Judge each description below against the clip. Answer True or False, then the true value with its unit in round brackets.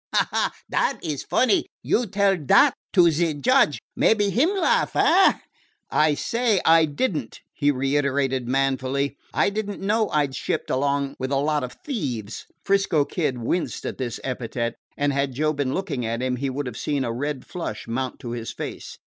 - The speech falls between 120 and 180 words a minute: False (190 wpm)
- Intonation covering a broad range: True (6.4 semitones)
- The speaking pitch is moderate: True (145 Hz)